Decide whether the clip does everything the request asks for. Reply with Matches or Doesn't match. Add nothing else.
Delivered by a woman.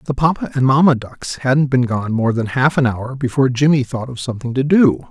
Doesn't match